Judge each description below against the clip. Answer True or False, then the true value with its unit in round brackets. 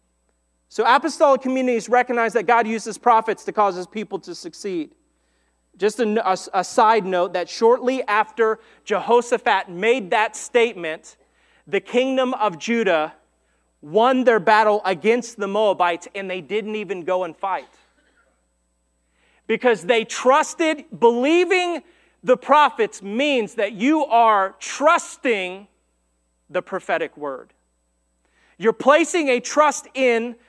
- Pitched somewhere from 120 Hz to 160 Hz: False (220 Hz)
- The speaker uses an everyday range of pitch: False (5.9 semitones)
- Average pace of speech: False (125 wpm)